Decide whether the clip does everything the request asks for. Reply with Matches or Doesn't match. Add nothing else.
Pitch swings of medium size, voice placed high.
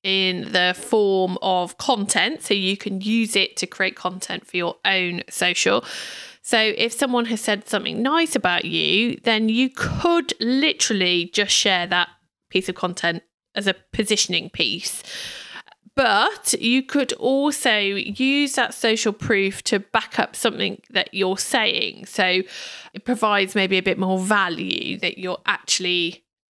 Matches